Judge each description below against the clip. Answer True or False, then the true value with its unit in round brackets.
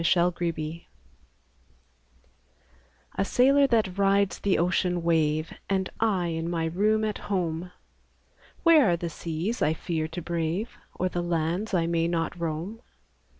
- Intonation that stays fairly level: False (3.2 semitones)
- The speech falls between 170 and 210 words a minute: False (140 wpm)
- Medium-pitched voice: True (175 Hz)